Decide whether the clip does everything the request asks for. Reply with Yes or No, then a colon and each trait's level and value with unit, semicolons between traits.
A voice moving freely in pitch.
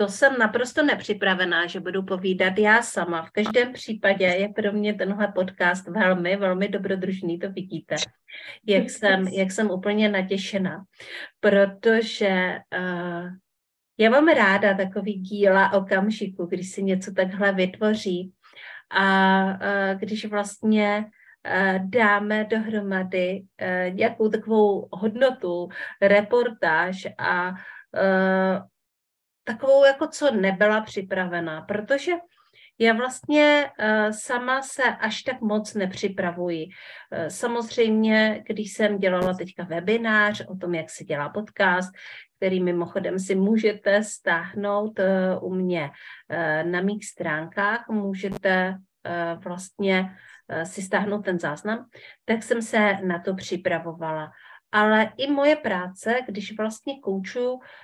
No: average, 2.7 semitones